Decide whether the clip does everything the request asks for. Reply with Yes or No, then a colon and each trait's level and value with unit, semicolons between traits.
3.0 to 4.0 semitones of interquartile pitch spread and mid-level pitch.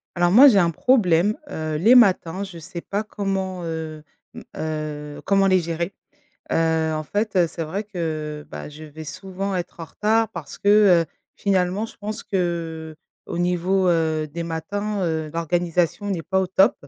Yes: average, 3.5 semitones; medium, 175 Hz